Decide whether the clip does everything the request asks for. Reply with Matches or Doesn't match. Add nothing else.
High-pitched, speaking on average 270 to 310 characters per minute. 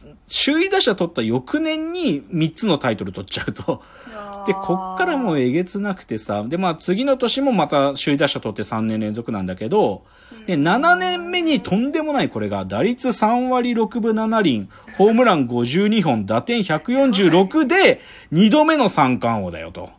Matches